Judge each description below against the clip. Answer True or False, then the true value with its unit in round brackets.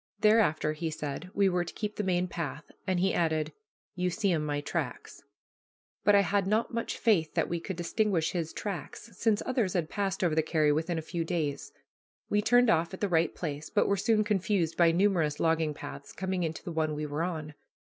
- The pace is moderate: False (210 wpm)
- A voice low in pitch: False (175 Hz)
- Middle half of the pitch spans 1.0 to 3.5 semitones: False (4.0 semitones)